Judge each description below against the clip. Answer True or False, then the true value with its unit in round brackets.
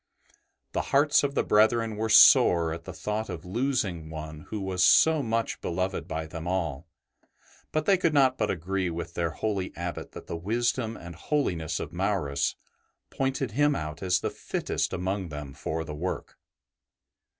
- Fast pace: False (170 wpm)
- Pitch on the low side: True (95 Hz)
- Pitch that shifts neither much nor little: False (5.7 semitones)